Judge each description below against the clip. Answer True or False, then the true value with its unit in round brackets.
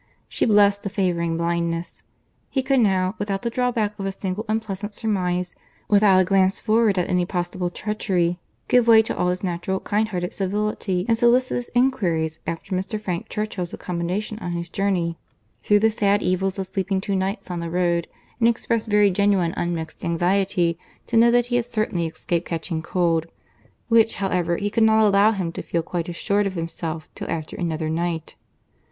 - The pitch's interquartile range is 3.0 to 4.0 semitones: True (3.5 semitones)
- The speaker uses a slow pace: False (185 wpm)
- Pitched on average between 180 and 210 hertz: True (190 Hz)